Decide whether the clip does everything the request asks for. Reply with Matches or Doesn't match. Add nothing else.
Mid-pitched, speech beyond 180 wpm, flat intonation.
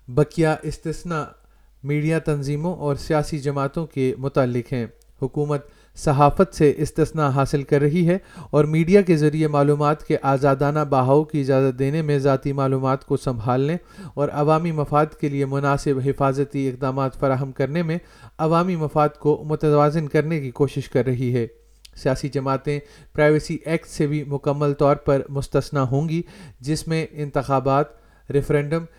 Doesn't match